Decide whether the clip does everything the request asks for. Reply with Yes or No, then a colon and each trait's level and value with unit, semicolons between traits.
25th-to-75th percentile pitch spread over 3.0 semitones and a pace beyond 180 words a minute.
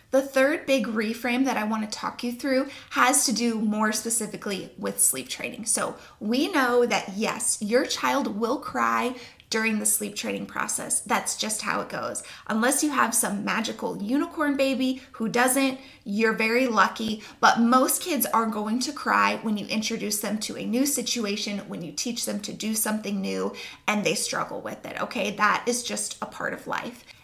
Yes: average, 3.4 semitones; average, 190 wpm